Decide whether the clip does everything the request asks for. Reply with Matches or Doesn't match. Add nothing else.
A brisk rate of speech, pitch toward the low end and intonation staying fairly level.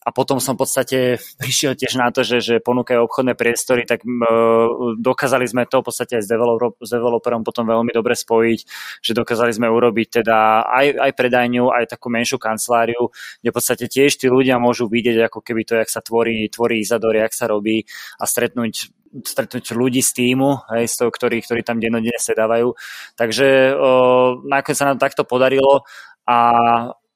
Matches